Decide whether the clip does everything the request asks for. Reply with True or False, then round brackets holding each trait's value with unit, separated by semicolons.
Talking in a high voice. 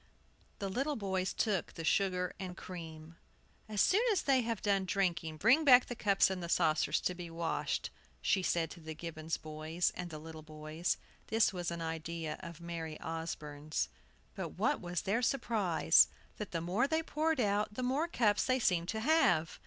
False (180 Hz)